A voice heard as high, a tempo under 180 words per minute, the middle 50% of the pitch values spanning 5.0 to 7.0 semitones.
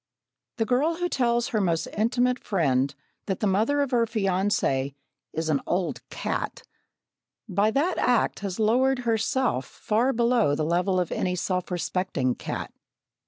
Yes: high, 210 Hz; average, 150 wpm; wide, 5.5 semitones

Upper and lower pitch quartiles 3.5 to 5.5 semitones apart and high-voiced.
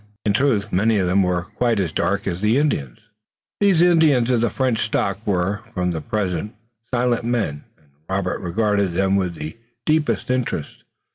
No: average, 5.0 semitones; low, 105 Hz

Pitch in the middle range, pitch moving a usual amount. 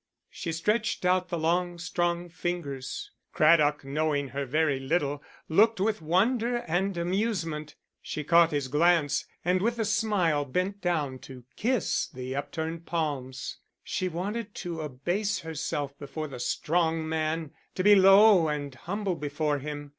Yes: medium, 165 Hz; average, 4.0 semitones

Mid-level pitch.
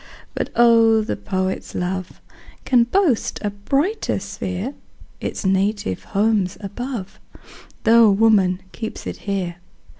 No: high, 205 Hz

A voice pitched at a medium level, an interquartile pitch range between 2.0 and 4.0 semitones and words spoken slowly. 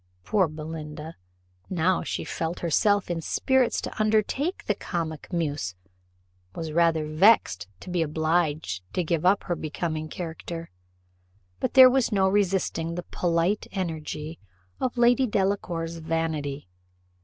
Yes: medium, 170 Hz; average, 3.7 semitones; slow, 130 wpm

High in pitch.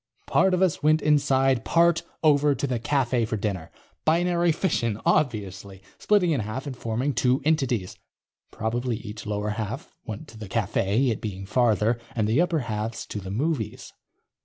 No: low, 120 Hz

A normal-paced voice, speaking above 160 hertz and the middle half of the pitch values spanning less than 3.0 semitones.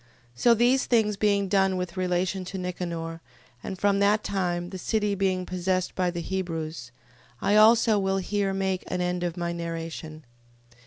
Yes: average, 170 wpm; medium, 185 Hz; narrow, 2.4 semitones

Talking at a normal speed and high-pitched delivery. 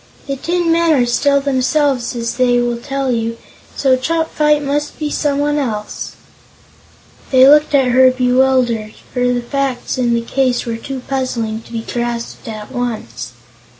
Yes: average, 160 wpm; very high, 255 Hz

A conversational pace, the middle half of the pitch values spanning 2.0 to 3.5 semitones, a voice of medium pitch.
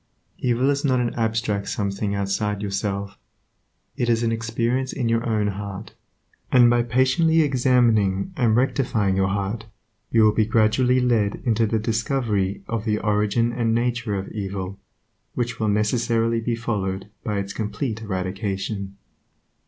No: average, 150 wpm; average, 2.9 semitones; low, 110 Hz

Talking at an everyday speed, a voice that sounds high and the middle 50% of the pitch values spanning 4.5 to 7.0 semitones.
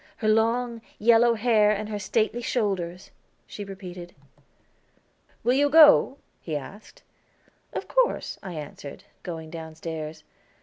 No: slow, 120 wpm; high, 210 Hz; wide, 5.4 semitones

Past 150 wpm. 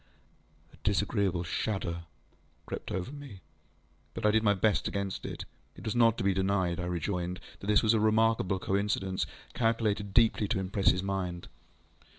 Yes: average, 165 wpm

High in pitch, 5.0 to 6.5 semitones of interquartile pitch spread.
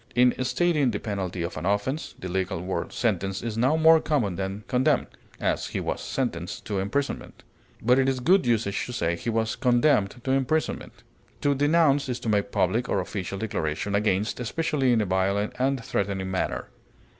No: low, 115 Hz; wide, 5.5 semitones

